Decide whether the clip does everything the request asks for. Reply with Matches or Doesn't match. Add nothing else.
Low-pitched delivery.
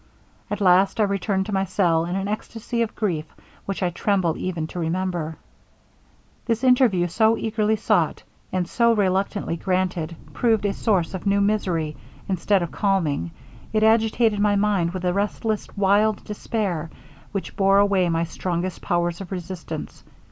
Doesn't match